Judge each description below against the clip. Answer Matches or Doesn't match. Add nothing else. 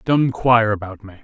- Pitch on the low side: Matches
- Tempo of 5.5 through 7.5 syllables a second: Matches